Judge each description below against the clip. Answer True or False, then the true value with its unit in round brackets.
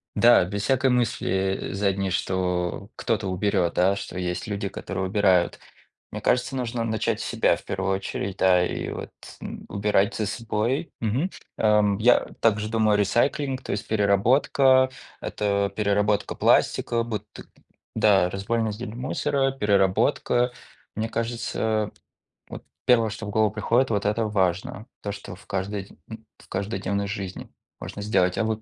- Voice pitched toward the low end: True (105 Hz)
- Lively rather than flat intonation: False (2.8 semitones)